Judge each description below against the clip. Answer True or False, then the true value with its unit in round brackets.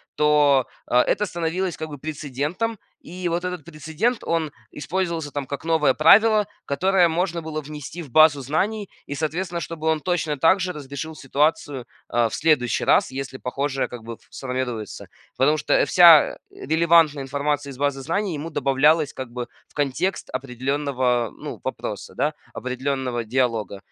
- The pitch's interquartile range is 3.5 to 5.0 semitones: True (3.8 semitones)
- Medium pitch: True (150 Hz)